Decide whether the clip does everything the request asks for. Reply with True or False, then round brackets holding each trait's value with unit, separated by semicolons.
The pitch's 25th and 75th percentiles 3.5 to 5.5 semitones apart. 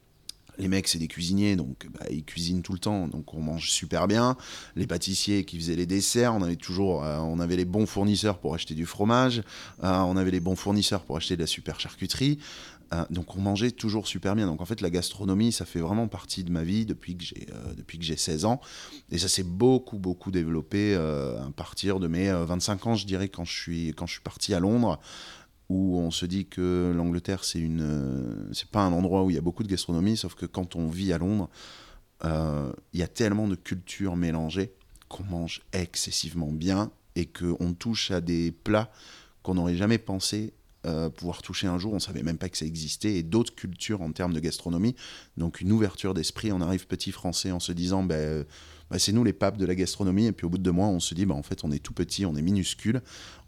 False (3.0 semitones)